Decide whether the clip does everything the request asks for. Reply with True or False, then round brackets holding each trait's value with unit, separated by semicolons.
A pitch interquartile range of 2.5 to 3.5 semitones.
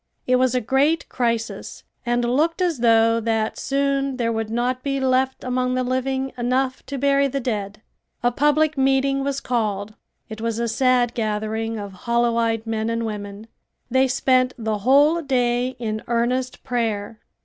True (2.9 semitones)